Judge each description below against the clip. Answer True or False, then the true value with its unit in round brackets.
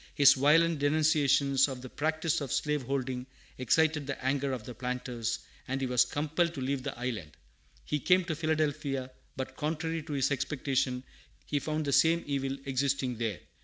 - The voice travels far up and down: False (3.0 semitones)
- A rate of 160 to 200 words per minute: True (165 wpm)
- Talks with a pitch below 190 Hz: True (140 Hz)